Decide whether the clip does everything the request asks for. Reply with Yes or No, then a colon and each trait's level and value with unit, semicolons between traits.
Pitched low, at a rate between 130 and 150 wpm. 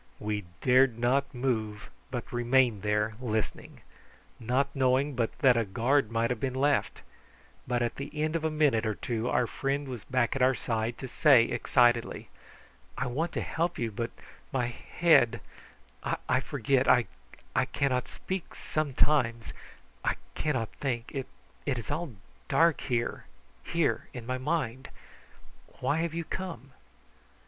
Yes: low, 125 Hz; average, 145 wpm